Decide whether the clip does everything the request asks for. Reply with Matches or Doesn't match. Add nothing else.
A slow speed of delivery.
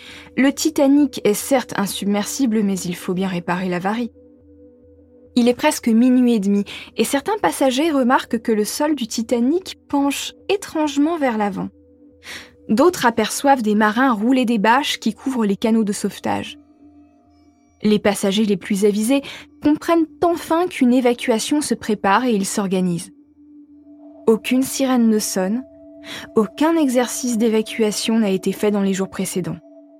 Matches